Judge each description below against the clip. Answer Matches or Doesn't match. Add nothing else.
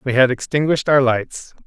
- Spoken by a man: Matches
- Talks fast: Doesn't match